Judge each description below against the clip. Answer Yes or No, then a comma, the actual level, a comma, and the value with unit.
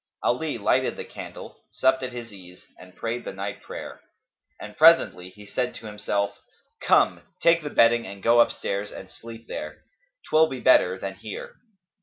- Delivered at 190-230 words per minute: No, average, 170 wpm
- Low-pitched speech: Yes, low, 110 Hz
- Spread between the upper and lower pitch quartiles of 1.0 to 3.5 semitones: No, average, 3.9 semitones